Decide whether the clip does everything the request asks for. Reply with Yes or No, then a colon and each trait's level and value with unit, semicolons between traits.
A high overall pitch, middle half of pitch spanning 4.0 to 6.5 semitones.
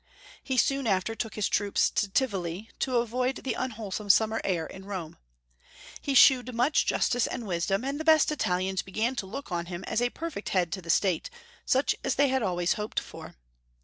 Yes: high, 215 Hz; wide, 5.4 semitones